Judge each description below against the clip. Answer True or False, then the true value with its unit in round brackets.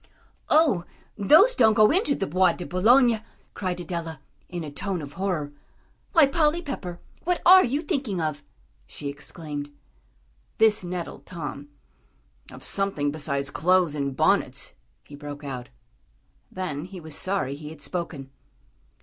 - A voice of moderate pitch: True (180 Hz)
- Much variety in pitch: True (6.7 semitones)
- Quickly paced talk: False (140 wpm)